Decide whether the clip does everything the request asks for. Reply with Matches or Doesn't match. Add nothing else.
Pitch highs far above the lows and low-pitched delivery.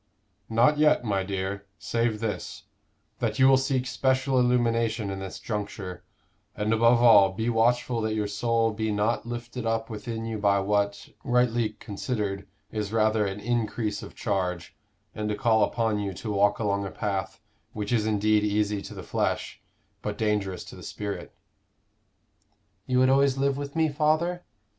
Doesn't match